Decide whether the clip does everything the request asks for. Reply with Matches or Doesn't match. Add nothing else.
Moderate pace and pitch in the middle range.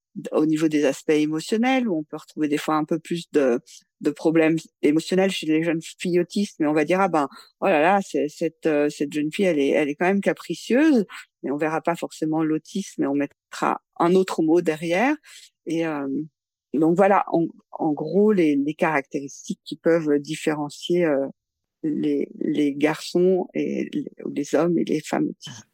Matches